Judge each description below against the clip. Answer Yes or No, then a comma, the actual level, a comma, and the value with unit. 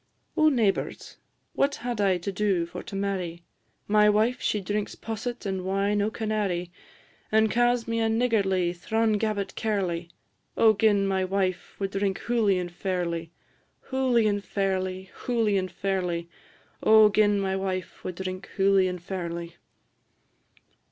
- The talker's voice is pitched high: Yes, high, 195 Hz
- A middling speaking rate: Yes, average, 145 wpm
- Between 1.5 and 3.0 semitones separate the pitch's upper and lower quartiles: Yes, average, 2.7 semitones